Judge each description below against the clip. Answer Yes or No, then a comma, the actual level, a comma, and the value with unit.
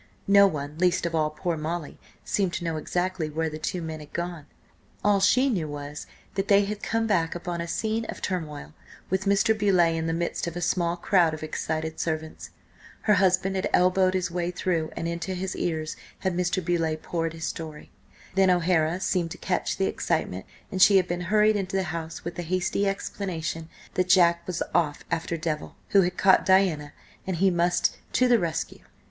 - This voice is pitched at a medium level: Yes, medium, 175 Hz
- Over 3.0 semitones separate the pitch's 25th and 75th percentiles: No, average, 2.7 semitones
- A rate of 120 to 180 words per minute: No, average, 200 wpm